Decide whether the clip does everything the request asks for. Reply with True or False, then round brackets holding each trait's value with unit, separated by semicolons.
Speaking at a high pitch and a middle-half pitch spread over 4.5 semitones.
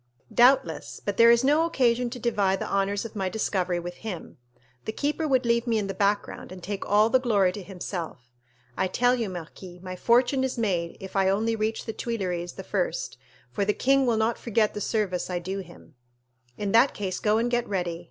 False (210 Hz; 4.0 semitones)